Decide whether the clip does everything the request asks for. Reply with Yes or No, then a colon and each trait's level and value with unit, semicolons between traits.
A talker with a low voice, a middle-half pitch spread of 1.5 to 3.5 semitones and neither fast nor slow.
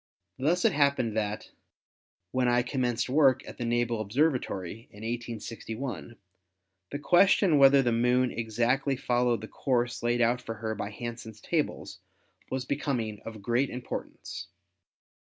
Yes: low, 120 Hz; average, 2.8 semitones; average, 145 wpm